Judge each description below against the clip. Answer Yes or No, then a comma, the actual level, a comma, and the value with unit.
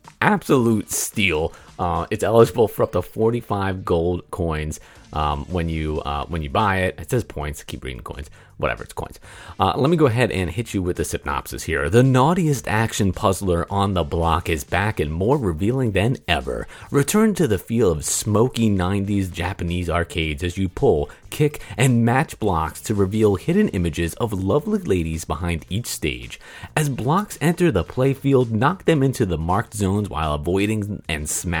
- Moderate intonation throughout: No, wide, 6.0 semitones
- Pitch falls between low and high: No, low, 100 Hz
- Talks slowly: No, average, 180 wpm